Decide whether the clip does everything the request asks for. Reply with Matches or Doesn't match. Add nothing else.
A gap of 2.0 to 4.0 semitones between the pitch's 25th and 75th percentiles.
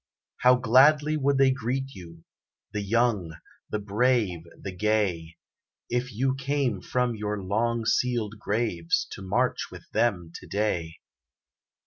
Doesn't match